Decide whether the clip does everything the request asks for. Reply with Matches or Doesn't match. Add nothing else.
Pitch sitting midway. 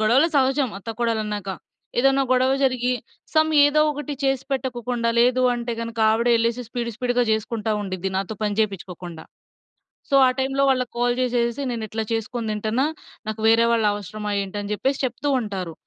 Doesn't match